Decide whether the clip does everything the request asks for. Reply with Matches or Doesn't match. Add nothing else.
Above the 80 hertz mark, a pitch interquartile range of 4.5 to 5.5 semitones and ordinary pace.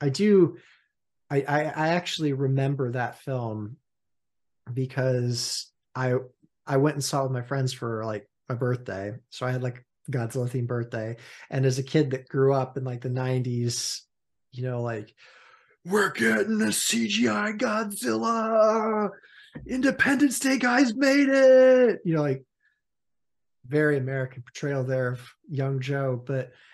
Matches